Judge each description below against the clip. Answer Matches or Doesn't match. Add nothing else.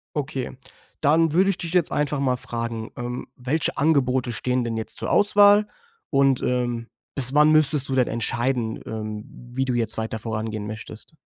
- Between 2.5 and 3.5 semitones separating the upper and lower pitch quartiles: Doesn't match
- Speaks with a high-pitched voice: Doesn't match